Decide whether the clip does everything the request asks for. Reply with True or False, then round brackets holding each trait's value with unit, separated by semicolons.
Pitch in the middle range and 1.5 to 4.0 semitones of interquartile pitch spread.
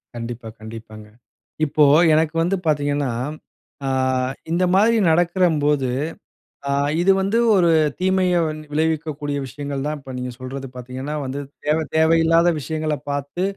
True (150 Hz; 3.6 semitones)